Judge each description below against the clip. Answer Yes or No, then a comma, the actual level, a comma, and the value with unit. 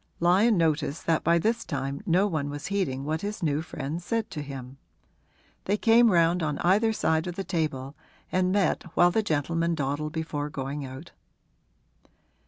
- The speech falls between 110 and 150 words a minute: No, average, 170 wpm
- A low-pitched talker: No, medium, 165 Hz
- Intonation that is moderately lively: Yes, average, 4.2 semitones